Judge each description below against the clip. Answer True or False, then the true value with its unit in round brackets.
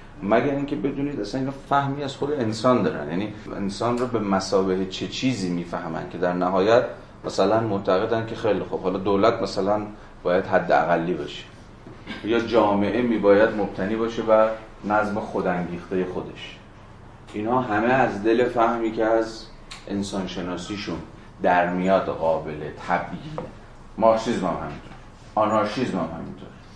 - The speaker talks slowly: False (140 wpm)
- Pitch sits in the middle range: False (105 Hz)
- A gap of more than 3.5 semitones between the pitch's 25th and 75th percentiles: False (3.1 semitones)